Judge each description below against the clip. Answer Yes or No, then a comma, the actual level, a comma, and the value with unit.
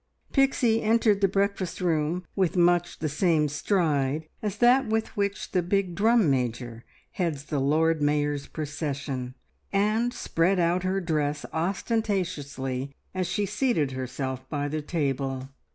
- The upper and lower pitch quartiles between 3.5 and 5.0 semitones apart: No, wide, 5.5 semitones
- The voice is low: No, medium, 165 Hz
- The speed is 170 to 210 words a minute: No, slow, 135 wpm